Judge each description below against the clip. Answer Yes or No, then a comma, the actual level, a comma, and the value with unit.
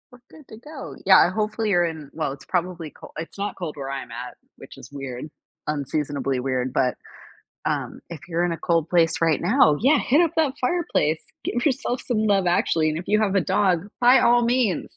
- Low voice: No, medium, 175 Hz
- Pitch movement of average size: No, wide, 7.1 semitones